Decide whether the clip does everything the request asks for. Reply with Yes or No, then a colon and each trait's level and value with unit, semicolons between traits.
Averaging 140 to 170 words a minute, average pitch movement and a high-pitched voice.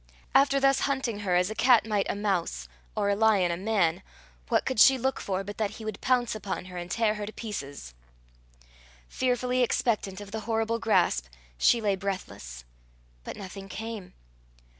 No: average, 180 wpm; average, 3.6 semitones; high, 210 Hz